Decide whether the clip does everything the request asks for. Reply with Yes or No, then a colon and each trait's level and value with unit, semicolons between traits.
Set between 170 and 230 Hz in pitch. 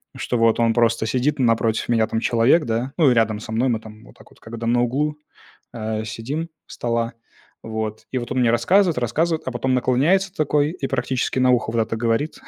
No: low, 120 Hz